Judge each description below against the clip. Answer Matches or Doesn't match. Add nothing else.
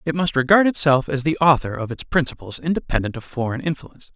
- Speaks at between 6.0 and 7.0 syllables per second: Matches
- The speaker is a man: Matches